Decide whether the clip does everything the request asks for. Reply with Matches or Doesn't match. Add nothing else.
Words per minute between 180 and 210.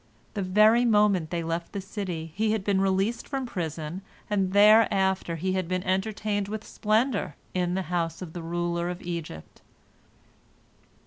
Doesn't match